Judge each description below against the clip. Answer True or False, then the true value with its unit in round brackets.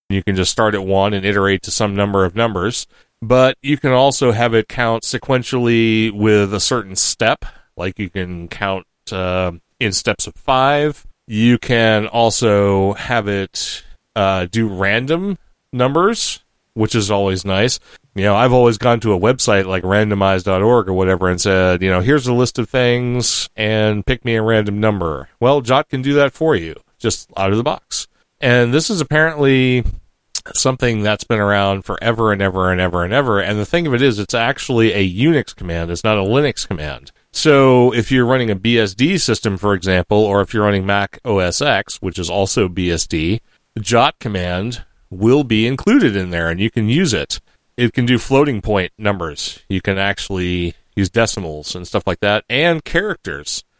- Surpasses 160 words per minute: True (185 wpm)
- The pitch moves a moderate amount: True (4.2 semitones)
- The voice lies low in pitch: True (110 Hz)